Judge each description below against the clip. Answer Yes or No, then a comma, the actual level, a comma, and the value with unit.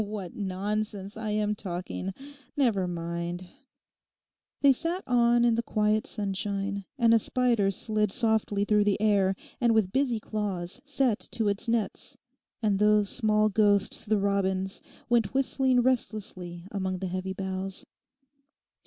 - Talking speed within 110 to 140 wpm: Yes, slow, 135 wpm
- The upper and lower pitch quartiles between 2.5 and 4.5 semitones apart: Yes, average, 3.1 semitones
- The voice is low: No, high, 210 Hz